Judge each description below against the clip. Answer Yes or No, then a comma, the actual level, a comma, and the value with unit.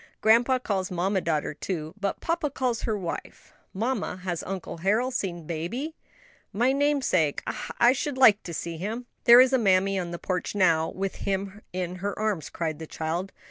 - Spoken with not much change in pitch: No, wide, 5.6 semitones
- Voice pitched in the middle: No, high, 195 Hz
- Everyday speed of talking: Yes, average, 180 wpm